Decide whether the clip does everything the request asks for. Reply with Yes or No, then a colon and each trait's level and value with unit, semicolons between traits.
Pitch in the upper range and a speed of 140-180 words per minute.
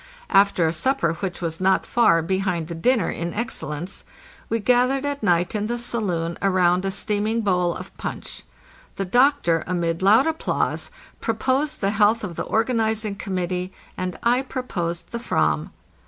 Yes: high, 195 Hz; average, 160 wpm